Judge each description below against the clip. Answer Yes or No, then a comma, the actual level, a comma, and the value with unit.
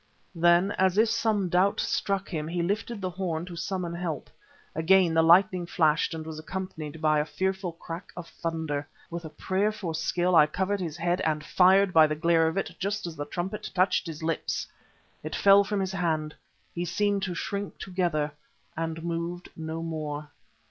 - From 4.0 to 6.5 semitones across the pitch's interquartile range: No, average, 2.9 semitones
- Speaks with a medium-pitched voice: Yes, medium, 175 Hz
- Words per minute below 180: No, average, 185 wpm